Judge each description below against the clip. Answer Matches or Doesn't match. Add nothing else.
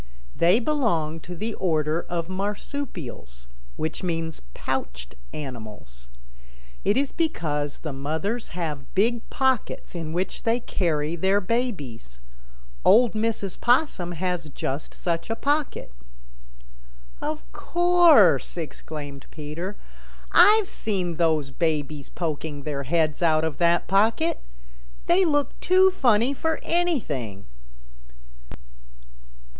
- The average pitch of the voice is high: Doesn't match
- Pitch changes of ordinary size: Doesn't match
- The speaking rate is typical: Doesn't match